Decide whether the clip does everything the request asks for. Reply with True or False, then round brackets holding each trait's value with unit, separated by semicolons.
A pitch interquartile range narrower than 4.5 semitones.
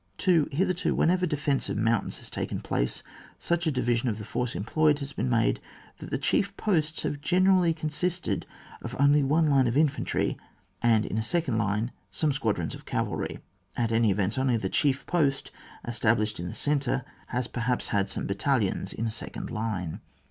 False (5.5 semitones)